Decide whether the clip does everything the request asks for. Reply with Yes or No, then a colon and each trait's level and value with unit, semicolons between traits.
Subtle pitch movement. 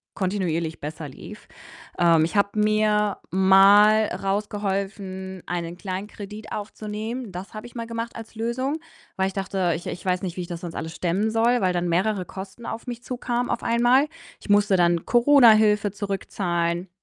No: average, 3.2 semitones